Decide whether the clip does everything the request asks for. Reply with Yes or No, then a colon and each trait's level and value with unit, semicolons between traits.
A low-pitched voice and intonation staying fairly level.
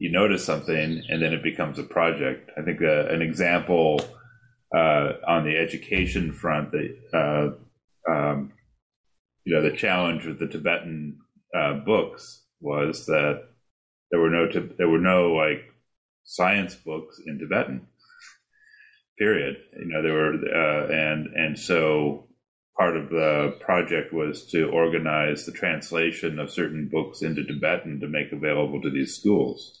Yes: very low, 80 Hz; narrow, 2.0 semitones